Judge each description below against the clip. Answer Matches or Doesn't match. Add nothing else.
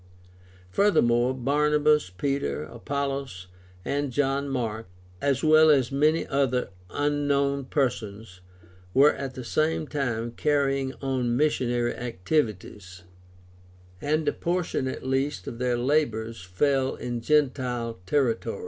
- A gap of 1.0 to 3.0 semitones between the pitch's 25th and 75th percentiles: Doesn't match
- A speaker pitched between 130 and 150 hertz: Matches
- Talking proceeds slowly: Matches